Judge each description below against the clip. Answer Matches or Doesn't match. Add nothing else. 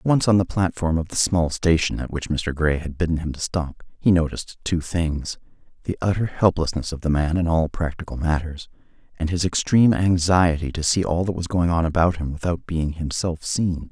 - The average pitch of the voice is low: Matches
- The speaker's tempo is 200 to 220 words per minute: Matches